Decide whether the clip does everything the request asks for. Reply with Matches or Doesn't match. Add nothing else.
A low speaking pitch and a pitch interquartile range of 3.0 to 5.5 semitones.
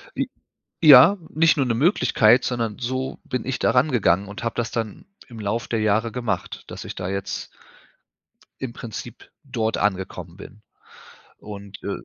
Matches